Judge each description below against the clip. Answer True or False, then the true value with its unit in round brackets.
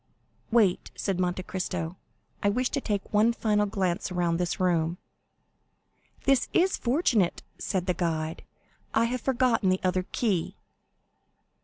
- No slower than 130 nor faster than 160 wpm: True (135 wpm)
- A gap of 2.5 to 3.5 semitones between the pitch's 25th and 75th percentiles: False (4.6 semitones)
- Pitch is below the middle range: False (190 Hz)